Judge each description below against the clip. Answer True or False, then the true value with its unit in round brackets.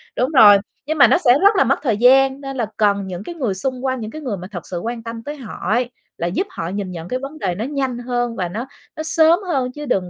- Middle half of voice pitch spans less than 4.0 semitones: False (5.2 semitones)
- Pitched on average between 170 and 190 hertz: False (245 Hz)